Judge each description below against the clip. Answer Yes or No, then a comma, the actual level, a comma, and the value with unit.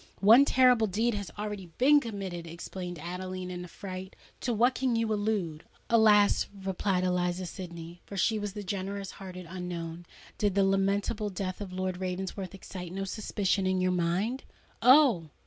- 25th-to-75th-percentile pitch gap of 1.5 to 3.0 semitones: Yes, narrow, 2.5 semitones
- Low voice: No, high, 190 Hz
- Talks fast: No, average, 150 wpm